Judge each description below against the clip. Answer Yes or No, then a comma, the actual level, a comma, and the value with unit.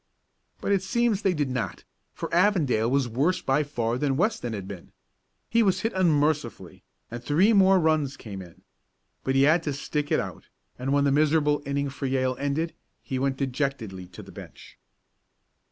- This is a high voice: No, medium, 140 Hz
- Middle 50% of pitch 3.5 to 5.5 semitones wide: Yes, average, 4.2 semitones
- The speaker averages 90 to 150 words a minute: No, average, 180 wpm